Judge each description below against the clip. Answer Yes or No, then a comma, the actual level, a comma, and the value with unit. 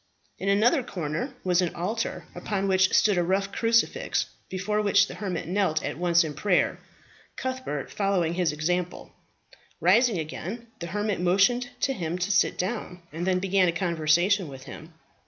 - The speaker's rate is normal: Yes, average, 165 wpm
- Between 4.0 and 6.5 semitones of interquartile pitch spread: No, average, 3.3 semitones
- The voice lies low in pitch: No, medium, 185 Hz